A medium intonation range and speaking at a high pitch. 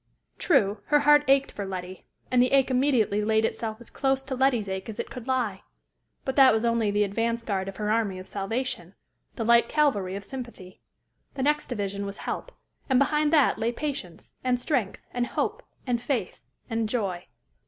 Yes: average, 4.7 semitones; high, 235 Hz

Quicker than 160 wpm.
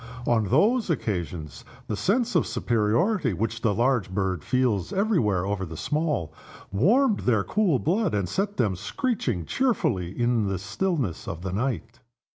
No: average, 155 wpm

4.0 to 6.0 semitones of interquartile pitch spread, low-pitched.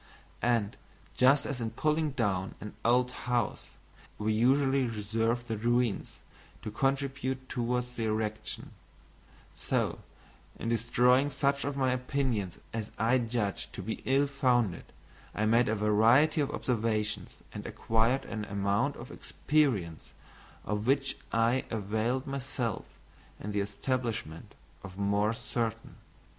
No: average, 3.5 semitones; low, 120 Hz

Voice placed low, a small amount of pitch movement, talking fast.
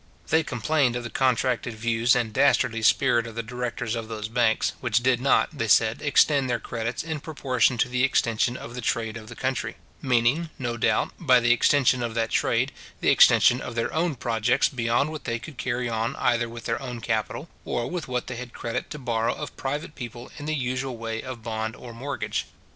Yes: low, 120 Hz; narrow, 2.2 semitones; fast, 210 wpm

